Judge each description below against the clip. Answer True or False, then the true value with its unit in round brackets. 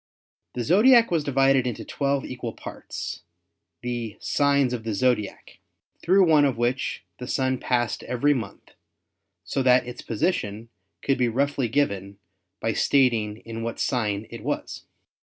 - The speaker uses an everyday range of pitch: True (3.5 semitones)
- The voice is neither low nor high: False (125 Hz)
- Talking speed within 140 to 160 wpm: True (150 wpm)